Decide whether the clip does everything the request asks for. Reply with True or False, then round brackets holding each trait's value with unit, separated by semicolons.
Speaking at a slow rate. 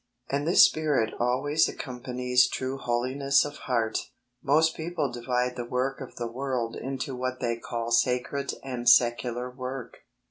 False (145 wpm)